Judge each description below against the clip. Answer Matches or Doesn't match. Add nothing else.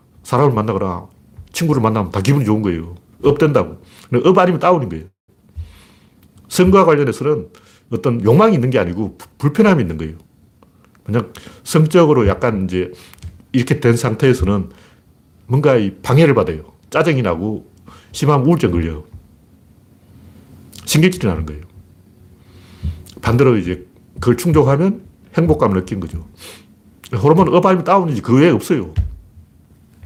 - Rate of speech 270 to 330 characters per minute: Matches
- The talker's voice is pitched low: Matches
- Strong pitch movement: Matches